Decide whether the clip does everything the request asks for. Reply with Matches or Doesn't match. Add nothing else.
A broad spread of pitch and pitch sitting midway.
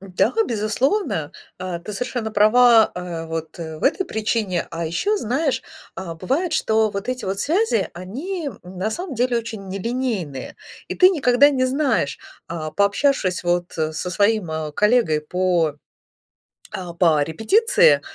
Doesn't match